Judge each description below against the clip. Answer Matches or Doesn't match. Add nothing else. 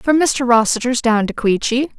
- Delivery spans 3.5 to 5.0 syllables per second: Matches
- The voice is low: Doesn't match